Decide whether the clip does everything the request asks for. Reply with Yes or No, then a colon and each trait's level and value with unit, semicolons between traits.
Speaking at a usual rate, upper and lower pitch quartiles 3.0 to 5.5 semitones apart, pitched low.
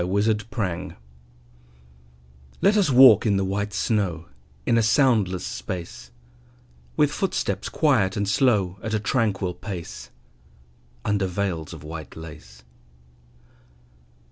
No: slow, 115 wpm; average, 3.8 semitones; low, 100 Hz